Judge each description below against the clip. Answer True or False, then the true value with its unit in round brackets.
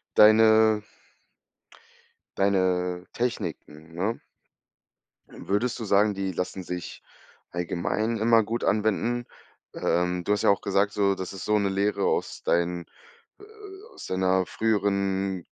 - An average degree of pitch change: True (3.0 semitones)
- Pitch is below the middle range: True (100 Hz)